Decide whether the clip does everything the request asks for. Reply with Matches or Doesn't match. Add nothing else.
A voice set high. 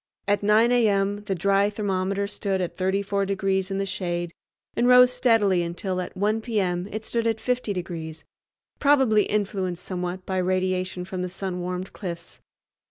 Matches